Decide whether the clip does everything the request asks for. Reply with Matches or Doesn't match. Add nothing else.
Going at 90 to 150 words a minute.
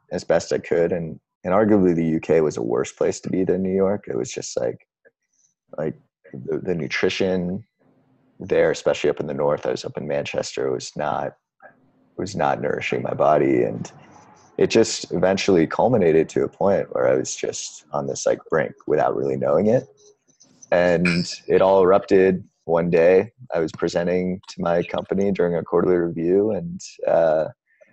Doesn't match